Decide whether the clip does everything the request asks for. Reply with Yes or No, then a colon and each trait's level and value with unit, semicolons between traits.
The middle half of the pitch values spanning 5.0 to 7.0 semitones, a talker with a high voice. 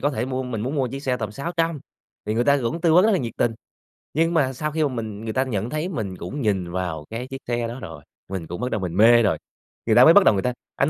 No: average, 5.3 semitones; low, 125 Hz